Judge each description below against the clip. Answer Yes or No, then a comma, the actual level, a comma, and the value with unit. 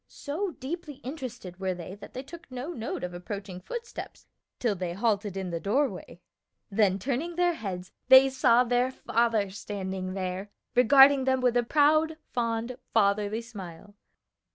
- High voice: Yes, high, 230 Hz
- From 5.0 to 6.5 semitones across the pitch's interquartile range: Yes, wide, 5.6 semitones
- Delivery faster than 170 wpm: No, average, 155 wpm